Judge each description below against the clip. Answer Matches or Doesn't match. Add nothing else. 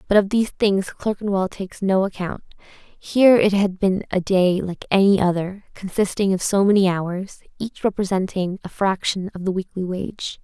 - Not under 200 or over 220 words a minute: Doesn't match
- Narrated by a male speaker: Doesn't match